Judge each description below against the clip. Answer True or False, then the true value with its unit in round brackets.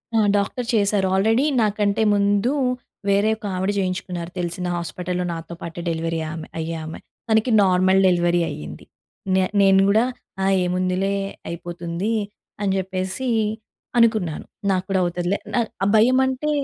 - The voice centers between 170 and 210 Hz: True (190 Hz)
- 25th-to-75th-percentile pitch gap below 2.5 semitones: False (2.8 semitones)